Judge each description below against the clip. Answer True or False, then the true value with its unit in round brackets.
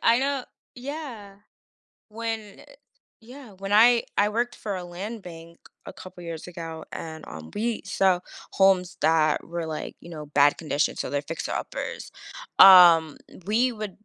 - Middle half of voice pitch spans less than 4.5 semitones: False (5.4 semitones)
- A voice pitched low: False (190 Hz)